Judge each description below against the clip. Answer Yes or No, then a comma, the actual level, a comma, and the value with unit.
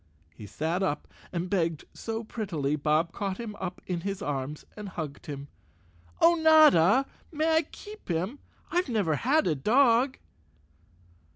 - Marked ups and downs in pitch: Yes, wide, 8.4 semitones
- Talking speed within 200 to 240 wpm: No, average, 150 wpm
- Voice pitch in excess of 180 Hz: Yes, high, 190 Hz